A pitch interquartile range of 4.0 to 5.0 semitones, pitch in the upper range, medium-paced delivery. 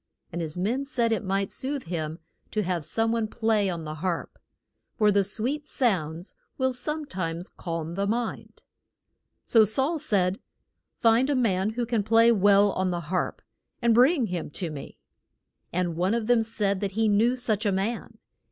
Yes: average, 4.4 semitones; high, 210 Hz; average, 175 wpm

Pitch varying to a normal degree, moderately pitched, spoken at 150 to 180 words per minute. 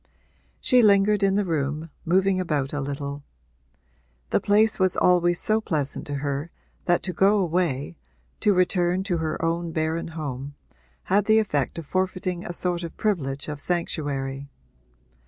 Yes: average, 4.5 semitones; medium, 170 Hz; average, 155 wpm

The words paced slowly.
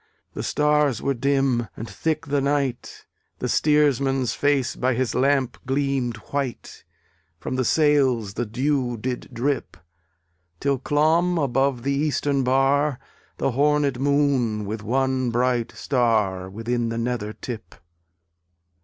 Yes: slow, 125 wpm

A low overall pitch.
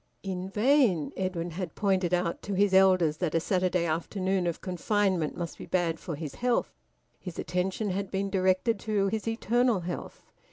No: medium, 185 Hz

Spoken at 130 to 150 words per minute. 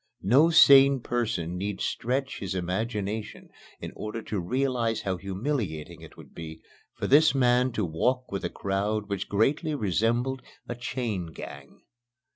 Yes: average, 145 wpm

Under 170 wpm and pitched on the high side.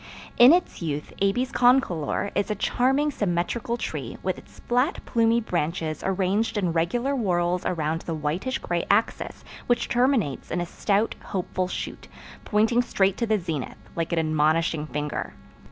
Yes: average, 155 wpm; high, 195 Hz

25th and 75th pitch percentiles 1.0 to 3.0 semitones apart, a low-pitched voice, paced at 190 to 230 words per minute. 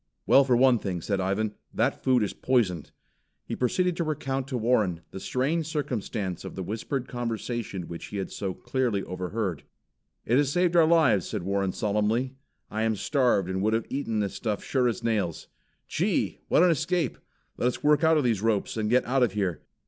No: average, 5.1 semitones; low, 115 Hz; average, 195 wpm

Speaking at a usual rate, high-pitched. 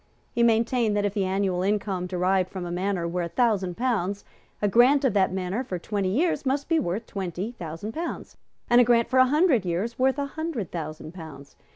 No: fast, 210 wpm; high, 205 Hz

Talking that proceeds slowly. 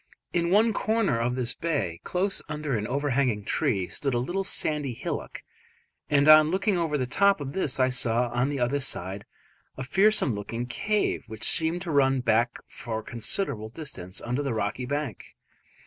No: average, 180 wpm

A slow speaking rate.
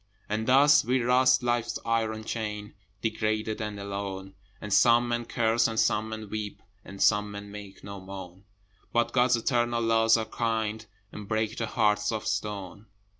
No: average, 165 wpm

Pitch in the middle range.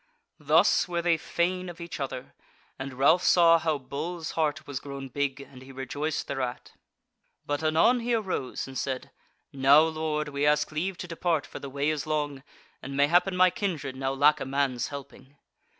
Yes: medium, 150 Hz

